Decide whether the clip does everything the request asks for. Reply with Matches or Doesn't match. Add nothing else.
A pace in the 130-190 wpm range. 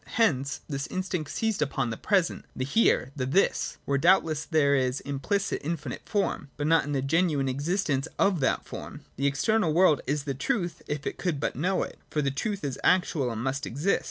Doesn't match